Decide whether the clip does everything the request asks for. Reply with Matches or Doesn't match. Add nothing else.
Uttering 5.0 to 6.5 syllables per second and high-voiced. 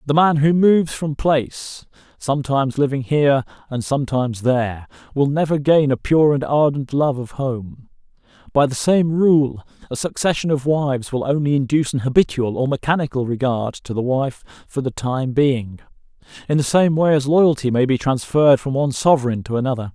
Doesn't match